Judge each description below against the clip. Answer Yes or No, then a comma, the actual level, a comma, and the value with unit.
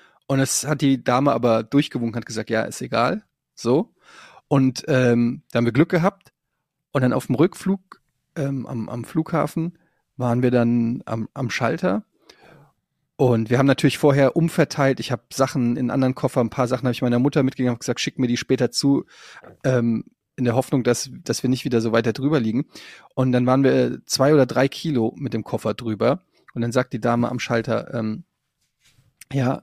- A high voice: No, low, 130 Hz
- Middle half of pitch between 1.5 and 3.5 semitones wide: Yes, narrow, 2.6 semitones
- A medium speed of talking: No, fast, 195 wpm